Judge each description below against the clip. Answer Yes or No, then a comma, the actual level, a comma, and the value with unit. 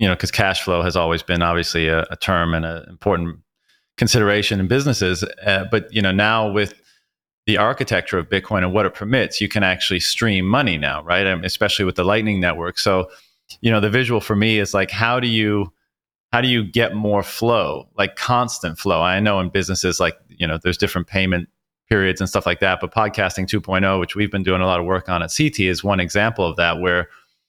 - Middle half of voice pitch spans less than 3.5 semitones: Yes, average, 2.9 semitones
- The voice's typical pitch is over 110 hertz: No, very low, 95 Hz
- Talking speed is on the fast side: Yes, fast, 225 wpm